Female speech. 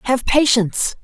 Yes: female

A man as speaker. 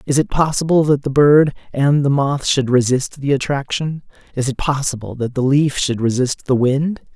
Yes: male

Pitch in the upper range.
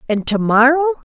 Yes: very high, 250 Hz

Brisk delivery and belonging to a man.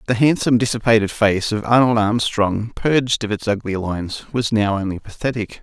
No: average, 170 wpm; male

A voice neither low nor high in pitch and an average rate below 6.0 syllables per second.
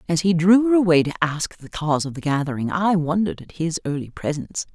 No: medium, 165 Hz; 6.2 syllables/s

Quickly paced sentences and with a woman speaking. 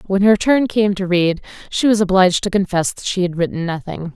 Yes: fast, 215 wpm; female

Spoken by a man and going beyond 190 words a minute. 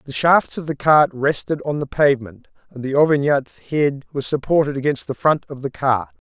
Yes: male; average, 200 wpm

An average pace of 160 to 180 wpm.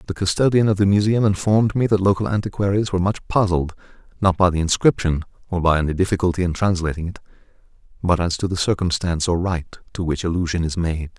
No: average, 195 wpm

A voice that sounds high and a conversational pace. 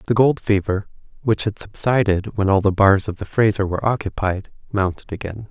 No: low, 100 Hz; average, 185 wpm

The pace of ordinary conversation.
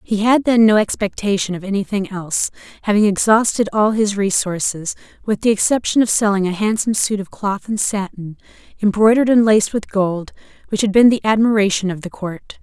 Yes: average, 180 wpm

